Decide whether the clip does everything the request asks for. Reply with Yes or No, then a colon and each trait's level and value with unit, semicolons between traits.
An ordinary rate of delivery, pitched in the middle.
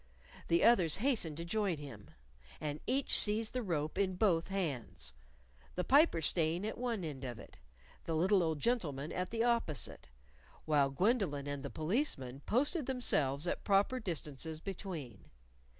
Yes: average, 150 wpm; medium, 170 Hz